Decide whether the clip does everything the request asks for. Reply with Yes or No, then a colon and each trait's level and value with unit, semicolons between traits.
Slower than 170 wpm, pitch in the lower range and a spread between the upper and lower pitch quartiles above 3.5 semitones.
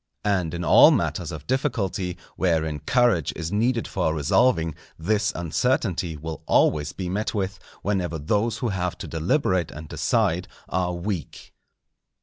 Yes: average, 140 wpm; very low, 90 Hz; average, 4.3 semitones